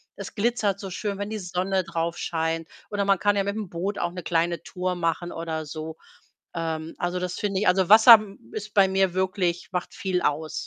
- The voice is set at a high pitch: No, medium, 180 Hz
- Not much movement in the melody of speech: No, average, 3.0 semitones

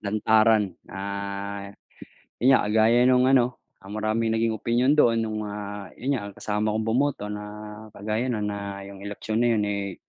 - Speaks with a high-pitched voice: No, low, 110 Hz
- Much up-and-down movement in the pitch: No, narrow, 2.4 semitones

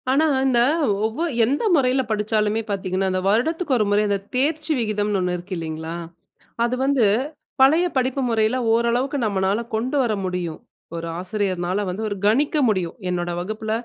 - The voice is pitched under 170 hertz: No, high, 215 Hz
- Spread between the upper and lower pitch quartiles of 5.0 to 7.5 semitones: Yes, average, 5.3 semitones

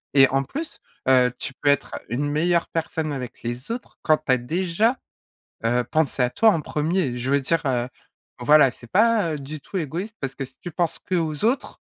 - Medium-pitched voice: Yes, medium, 150 Hz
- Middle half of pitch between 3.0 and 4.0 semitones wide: No, average, 4.8 semitones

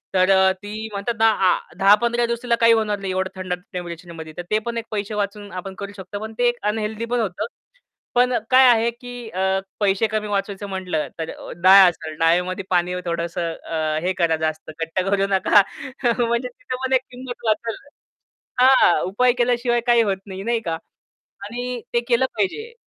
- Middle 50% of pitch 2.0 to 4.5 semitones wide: Yes, average, 4.2 semitones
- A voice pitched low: No, high, 205 Hz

